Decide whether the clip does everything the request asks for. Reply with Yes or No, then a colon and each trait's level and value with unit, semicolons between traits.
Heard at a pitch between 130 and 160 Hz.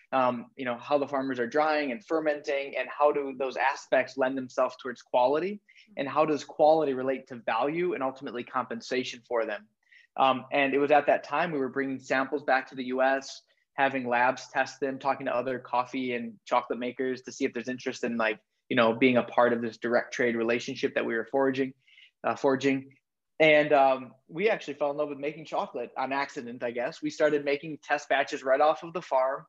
Yes: low, 135 Hz